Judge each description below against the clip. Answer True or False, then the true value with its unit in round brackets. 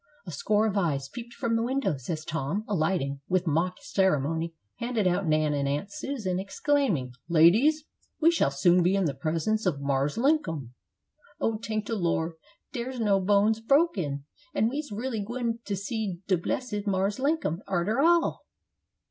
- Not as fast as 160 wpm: False (165 wpm)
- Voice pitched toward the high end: True (195 Hz)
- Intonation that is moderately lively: False (6.1 semitones)